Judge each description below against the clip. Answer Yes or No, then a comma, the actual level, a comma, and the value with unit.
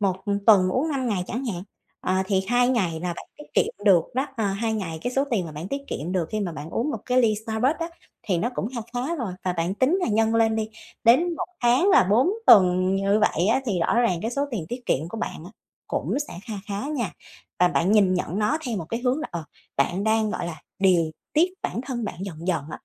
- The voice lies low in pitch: No, high, 210 Hz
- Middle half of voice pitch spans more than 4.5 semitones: Yes, average, 5.2 semitones